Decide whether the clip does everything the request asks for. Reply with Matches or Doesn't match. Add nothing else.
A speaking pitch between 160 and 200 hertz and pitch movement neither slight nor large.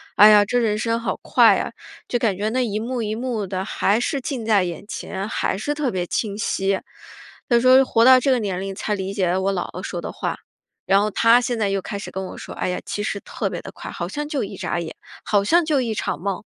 Doesn't match